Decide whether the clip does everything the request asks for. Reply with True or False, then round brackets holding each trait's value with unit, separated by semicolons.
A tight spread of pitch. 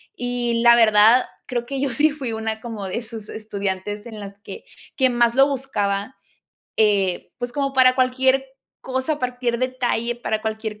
False (3.0 semitones)